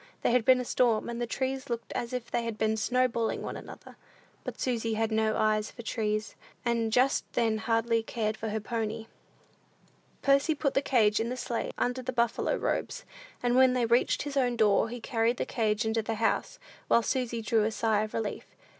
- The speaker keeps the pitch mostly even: Yes, narrow, 2.1 semitones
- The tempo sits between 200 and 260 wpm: Yes, fast, 205 wpm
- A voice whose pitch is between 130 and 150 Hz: No, high, 230 Hz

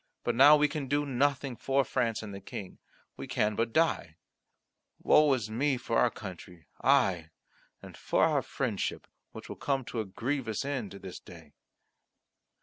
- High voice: No, low, 120 Hz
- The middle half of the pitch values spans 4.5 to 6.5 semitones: Yes, wide, 5.6 semitones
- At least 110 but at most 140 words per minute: No, average, 165 wpm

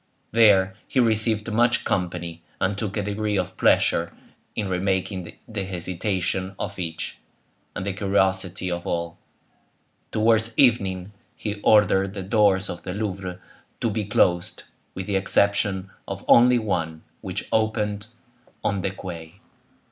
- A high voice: No, very low, 95 Hz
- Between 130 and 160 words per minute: Yes, slow, 135 wpm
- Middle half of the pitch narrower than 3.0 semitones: Yes, narrow, 2.5 semitones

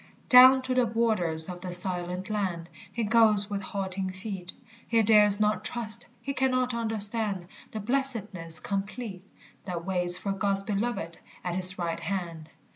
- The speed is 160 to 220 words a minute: No, average, 150 wpm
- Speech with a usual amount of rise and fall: Yes, average, 3.8 semitones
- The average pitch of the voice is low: No, high, 200 Hz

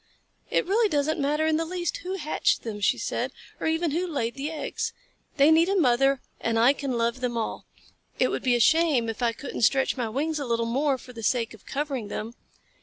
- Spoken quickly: Yes, fast, 225 wpm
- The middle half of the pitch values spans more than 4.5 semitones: Yes, average, 5.1 semitones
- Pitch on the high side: Yes, very high, 275 Hz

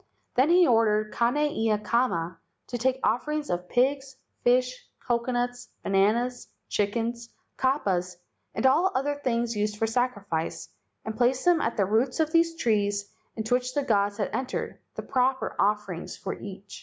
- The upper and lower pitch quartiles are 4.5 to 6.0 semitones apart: No, average, 3.9 semitones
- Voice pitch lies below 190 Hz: No, high, 235 Hz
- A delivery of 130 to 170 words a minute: Yes, average, 155 wpm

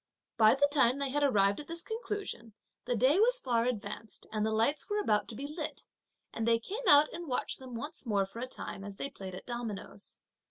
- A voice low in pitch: No, very high, 250 Hz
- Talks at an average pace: No, fast, 225 wpm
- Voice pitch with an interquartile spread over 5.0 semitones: Yes, wide, 5.4 semitones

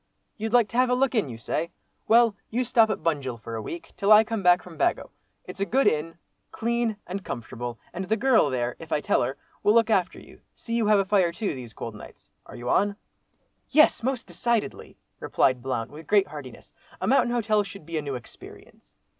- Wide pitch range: Yes, wide, 7.7 semitones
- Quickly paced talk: Yes, fast, 220 wpm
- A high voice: Yes, high, 195 Hz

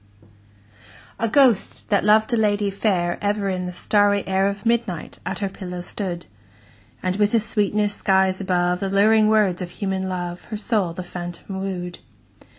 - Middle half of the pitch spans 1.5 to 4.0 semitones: Yes, narrow, 2.5 semitones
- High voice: Yes, high, 195 Hz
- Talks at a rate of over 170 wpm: No, average, 165 wpm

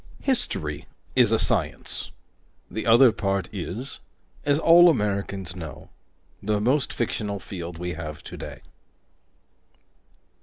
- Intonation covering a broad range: Yes, wide, 6.0 semitones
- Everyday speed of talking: No, slow, 110 wpm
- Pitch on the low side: Yes, low, 100 Hz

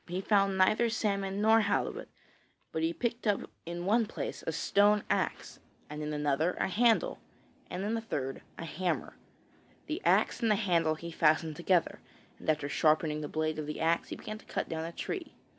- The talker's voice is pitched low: No, medium, 180 Hz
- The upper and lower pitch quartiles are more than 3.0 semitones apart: Yes, average, 5.2 semitones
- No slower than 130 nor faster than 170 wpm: No, average, 190 wpm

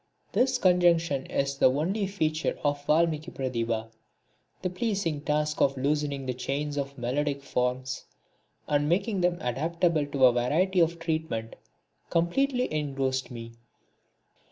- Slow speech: Yes, slow, 130 wpm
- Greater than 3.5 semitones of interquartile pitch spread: Yes, average, 4.3 semitones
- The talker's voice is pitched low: No, medium, 150 Hz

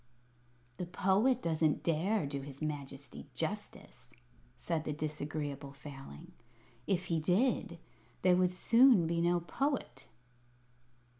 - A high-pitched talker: No, medium, 165 Hz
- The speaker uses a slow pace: Yes, slow, 115 wpm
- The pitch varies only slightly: No, average, 4.3 semitones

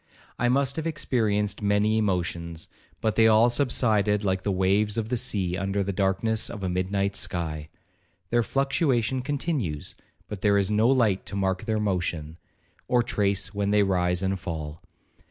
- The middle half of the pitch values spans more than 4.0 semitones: No, average, 3.2 semitones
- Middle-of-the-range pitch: No, low, 100 Hz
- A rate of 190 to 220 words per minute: No, average, 160 wpm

